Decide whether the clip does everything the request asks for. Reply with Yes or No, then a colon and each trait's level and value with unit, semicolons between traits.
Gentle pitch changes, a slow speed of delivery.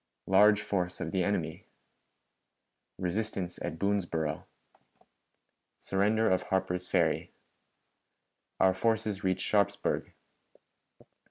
Yes: narrow, 2.2 semitones; slow, 85 wpm